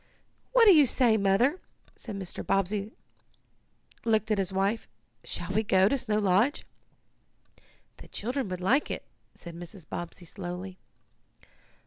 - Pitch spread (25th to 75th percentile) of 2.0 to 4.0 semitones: Yes, average, 3.7 semitones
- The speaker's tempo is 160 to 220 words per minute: No, slow, 135 wpm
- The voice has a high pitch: Yes, high, 200 Hz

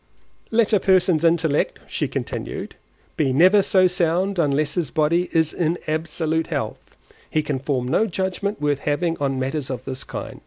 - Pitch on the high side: No, medium, 160 Hz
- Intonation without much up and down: No, average, 3.7 semitones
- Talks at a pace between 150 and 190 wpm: Yes, average, 165 wpm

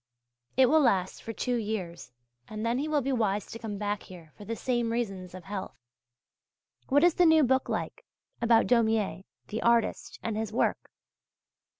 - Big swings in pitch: No, average, 3.4 semitones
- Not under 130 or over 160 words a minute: No, average, 180 wpm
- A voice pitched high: Yes, high, 225 Hz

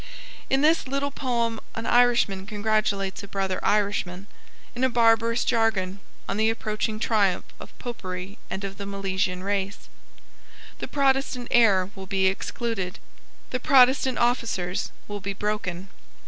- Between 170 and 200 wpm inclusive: No, slow, 135 wpm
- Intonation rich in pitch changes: No, average, 3.8 semitones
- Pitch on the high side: Yes, high, 210 Hz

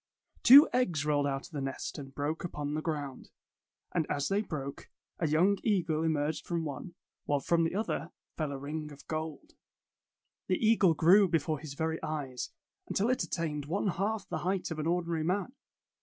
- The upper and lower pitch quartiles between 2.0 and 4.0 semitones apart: Yes, average, 3.7 semitones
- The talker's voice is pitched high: No, medium, 160 Hz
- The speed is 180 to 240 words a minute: Yes, average, 185 wpm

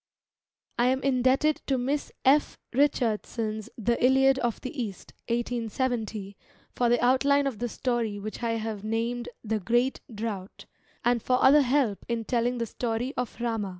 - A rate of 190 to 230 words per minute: No, average, 155 wpm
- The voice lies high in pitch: Yes, high, 240 Hz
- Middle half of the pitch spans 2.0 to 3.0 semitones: Yes, narrow, 2.6 semitones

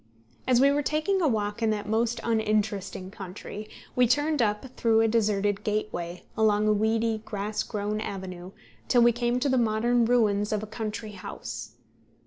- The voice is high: Yes, high, 215 Hz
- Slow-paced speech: No, average, 170 wpm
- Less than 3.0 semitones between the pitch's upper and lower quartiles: Yes, narrow, 2.5 semitones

